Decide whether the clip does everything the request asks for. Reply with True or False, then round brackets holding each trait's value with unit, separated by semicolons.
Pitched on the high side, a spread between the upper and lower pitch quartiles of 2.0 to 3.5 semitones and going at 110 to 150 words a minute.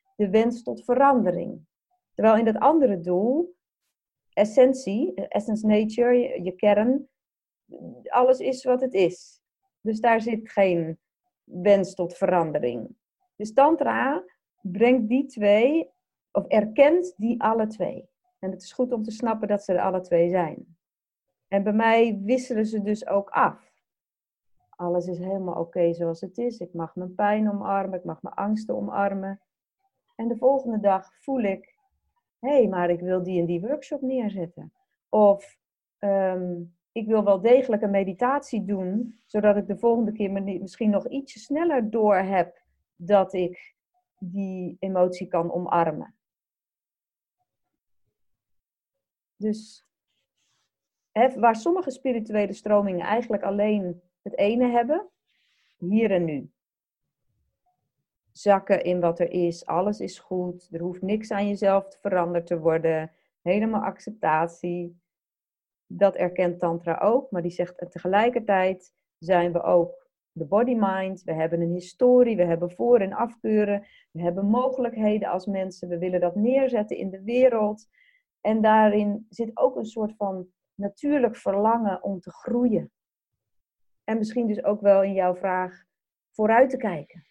False (205 Hz; 4.7 semitones; 145 wpm)